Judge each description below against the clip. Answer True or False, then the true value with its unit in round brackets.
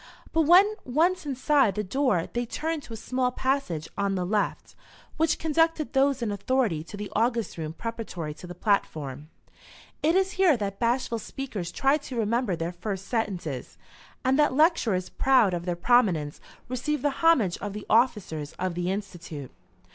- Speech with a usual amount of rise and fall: False (7.0 semitones)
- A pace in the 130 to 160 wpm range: False (170 wpm)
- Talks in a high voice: True (230 Hz)